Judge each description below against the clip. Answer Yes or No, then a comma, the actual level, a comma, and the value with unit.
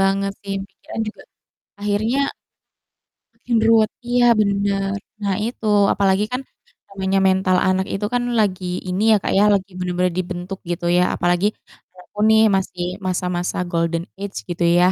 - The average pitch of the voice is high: Yes, high, 195 Hz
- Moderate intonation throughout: No, narrow, 2.0 semitones